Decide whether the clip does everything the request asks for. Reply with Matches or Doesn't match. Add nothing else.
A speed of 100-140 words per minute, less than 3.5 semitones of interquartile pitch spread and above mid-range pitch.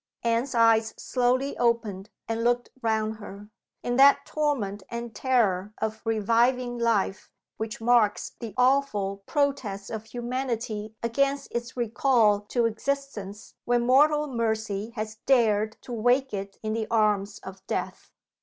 Matches